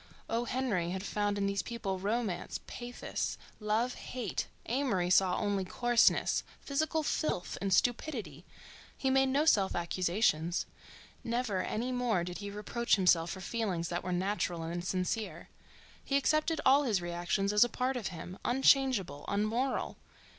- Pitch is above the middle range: Yes, high, 205 Hz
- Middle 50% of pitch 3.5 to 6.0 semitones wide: Yes, average, 5.3 semitones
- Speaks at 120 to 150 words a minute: Yes, average, 145 wpm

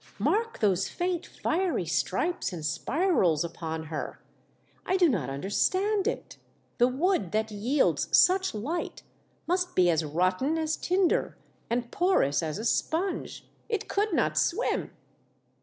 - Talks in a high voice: Yes, very high, 255 Hz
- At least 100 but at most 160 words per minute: Yes, average, 140 wpm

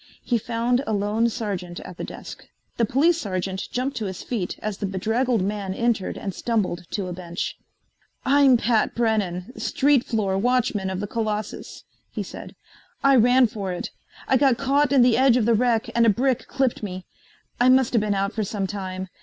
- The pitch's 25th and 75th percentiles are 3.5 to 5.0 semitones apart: Yes, average, 4.2 semitones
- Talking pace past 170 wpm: Yes, average, 190 wpm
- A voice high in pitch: Yes, high, 220 Hz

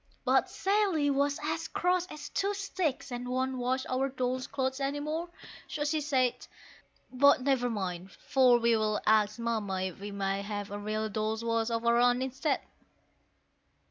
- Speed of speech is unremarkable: Yes, average, 165 wpm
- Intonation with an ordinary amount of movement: Yes, average, 4.7 semitones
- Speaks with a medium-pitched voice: No, very high, 255 Hz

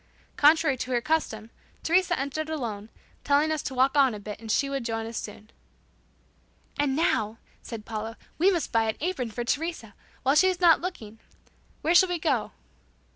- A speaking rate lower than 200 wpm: Yes, average, 180 wpm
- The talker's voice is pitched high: Yes, very high, 270 Hz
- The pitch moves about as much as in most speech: No, wide, 6.1 semitones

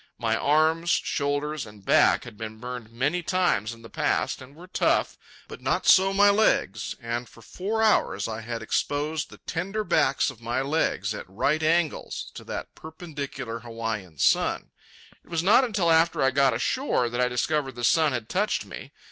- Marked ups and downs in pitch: Yes, wide, 6.2 semitones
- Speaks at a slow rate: No, average, 180 wpm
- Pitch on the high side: No, medium, 140 Hz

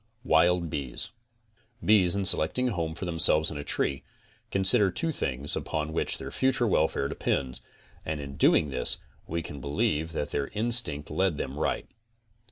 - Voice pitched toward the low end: Yes, very low, 80 Hz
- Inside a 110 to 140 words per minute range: No, average, 165 wpm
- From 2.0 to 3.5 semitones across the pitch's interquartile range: No, average, 4.9 semitones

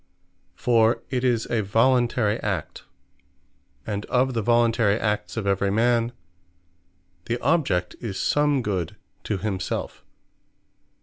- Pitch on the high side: No, low, 115 Hz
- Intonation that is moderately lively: Yes, average, 3.1 semitones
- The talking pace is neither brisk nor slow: No, slow, 115 wpm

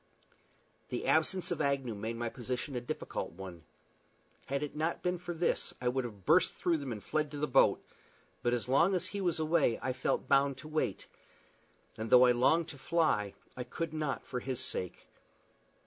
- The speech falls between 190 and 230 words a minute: Yes, average, 195 wpm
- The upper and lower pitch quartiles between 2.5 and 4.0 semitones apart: No, average, 4.5 semitones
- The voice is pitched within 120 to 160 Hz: Yes, medium, 140 Hz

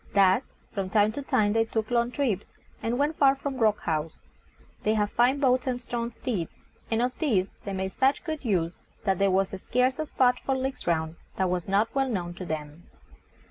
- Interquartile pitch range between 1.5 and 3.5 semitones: No, average, 5.3 semitones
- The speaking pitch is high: Yes, high, 220 Hz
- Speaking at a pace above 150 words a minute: Yes, fast, 205 wpm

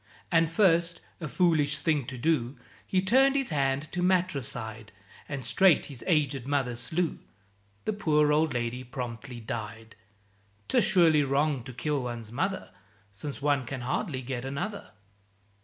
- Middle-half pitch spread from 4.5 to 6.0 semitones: Yes, average, 4.9 semitones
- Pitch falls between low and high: Yes, medium, 145 Hz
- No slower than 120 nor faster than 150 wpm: Yes, average, 145 wpm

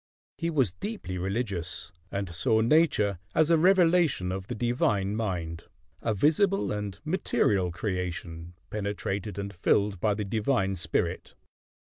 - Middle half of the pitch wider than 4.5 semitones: Yes, average, 5.3 semitones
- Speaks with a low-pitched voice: Yes, low, 100 Hz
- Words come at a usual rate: No, slow, 130 wpm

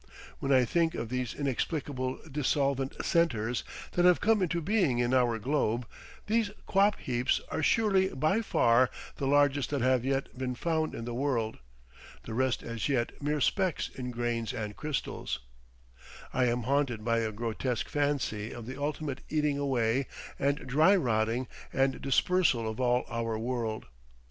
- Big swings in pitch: No, average, 3.9 semitones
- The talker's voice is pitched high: No, low, 130 Hz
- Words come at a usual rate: Yes, average, 155 wpm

